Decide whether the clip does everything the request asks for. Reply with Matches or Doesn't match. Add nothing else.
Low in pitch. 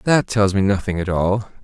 Matches